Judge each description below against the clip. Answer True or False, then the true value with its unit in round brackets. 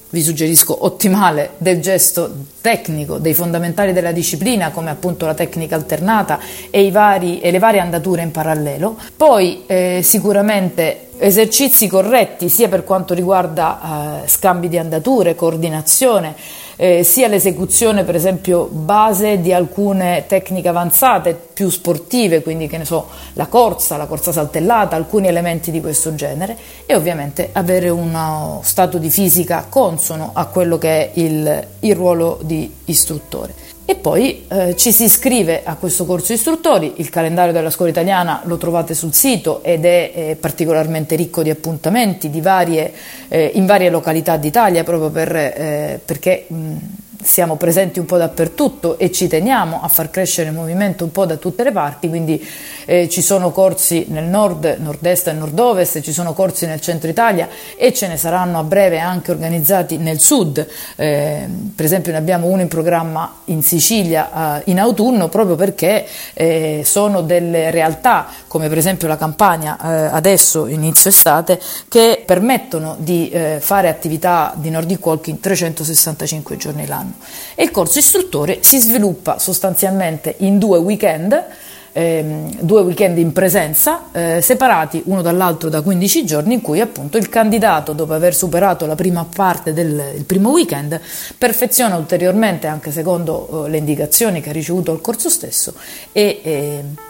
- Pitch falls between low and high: True (175 Hz)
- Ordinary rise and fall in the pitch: True (3.2 semitones)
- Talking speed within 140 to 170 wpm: True (160 wpm)